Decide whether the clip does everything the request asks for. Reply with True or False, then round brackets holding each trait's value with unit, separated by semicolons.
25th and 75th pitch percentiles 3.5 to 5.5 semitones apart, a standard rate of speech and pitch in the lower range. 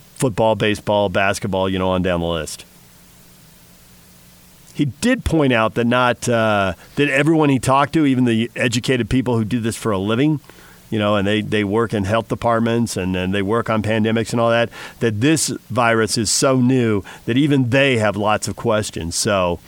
True (4.0 semitones; 190 wpm; 115 Hz)